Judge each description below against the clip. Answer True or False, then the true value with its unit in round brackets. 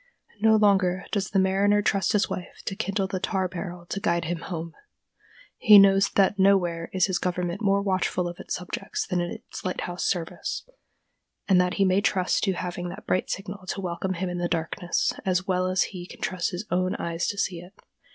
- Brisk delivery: True (210 wpm)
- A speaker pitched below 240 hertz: True (185 Hz)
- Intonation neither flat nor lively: False (1.8 semitones)